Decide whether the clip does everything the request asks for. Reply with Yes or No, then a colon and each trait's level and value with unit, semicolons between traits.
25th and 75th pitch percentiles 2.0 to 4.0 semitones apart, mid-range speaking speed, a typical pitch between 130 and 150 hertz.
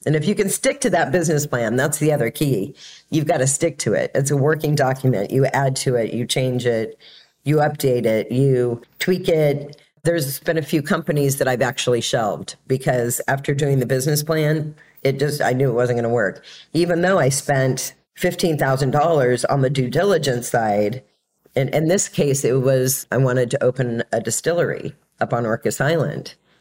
Yes: average, 3.3 semitones; average, 195 wpm; medium, 140 Hz